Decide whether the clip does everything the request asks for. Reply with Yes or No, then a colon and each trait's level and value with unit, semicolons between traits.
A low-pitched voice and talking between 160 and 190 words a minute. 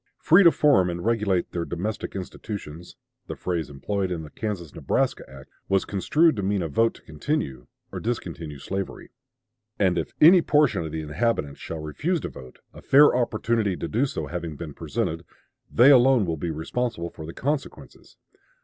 Yes: very low, 95 Hz; average, 175 wpm